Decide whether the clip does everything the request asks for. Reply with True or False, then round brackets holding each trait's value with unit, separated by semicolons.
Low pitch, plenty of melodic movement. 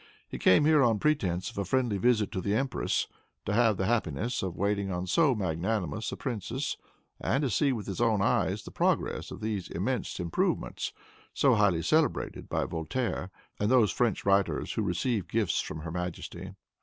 False (105 Hz; 4.8 semitones)